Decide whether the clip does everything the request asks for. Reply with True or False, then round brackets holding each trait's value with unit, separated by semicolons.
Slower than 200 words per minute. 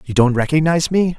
False (205 wpm)